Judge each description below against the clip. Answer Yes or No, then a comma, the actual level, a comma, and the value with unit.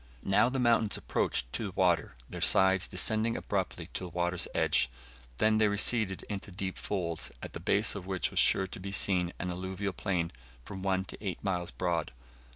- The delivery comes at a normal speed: Yes, average, 190 wpm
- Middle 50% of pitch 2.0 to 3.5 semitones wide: Yes, narrow, 2.4 semitones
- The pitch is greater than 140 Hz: No, very low, 95 Hz